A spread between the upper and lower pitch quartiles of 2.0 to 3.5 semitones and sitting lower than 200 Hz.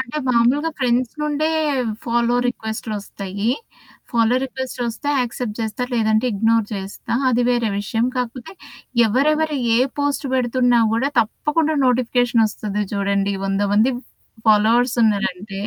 No: average, 2.9 semitones; high, 235 Hz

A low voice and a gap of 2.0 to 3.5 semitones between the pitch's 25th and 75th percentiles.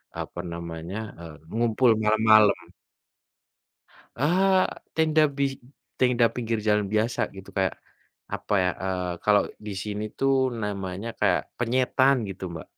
No: low, 110 Hz; average, 4.6 semitones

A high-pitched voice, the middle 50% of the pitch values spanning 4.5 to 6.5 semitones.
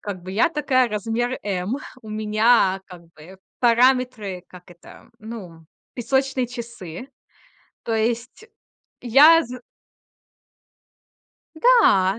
Yes: high, 230 Hz; average, 4.9 semitones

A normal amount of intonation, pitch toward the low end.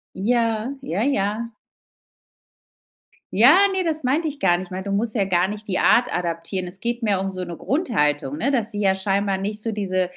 No: average, 4.1 semitones; high, 205 Hz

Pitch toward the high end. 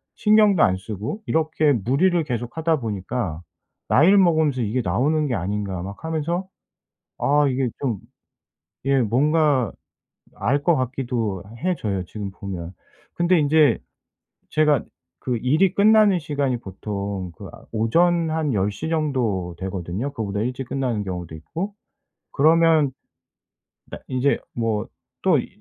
No: low, 130 Hz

